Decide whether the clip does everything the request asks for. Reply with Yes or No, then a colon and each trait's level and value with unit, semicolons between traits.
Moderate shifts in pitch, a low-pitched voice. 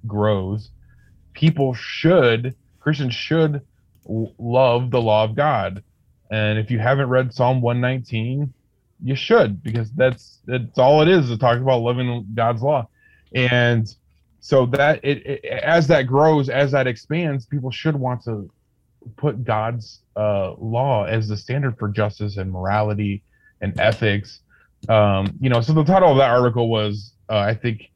Yes: average, 3.8 semitones; low, 120 Hz